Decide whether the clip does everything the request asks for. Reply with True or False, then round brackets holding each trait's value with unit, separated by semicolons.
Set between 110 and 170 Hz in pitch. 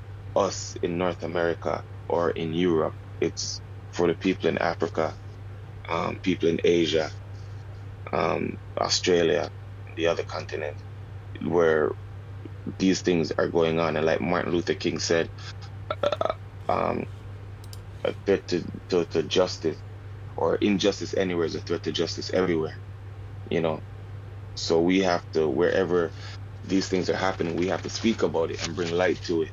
False (100 Hz)